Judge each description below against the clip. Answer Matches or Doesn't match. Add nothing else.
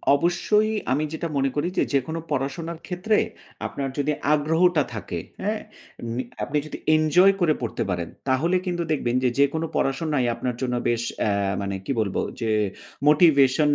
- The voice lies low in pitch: Doesn't match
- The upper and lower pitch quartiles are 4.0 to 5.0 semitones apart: Matches